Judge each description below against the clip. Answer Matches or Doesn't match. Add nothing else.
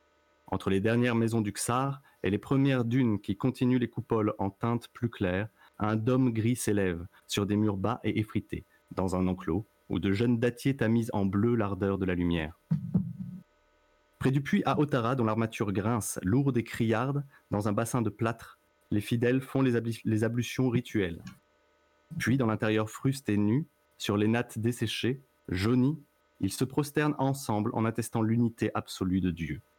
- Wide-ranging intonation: Doesn't match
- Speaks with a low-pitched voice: Matches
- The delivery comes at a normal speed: Matches